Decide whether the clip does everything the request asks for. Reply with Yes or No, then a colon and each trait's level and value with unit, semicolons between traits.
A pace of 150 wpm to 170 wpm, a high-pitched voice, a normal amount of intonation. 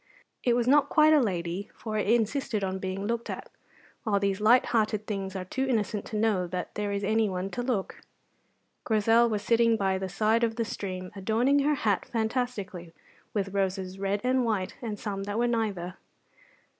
No: average, 185 wpm; high, 210 Hz; average, 3.2 semitones